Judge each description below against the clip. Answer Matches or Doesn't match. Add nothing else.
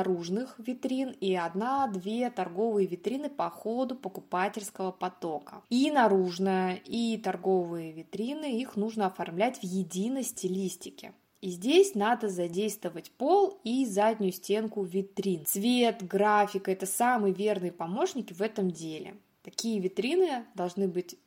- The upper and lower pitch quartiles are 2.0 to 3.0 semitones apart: Doesn't match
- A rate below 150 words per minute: Matches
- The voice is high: Matches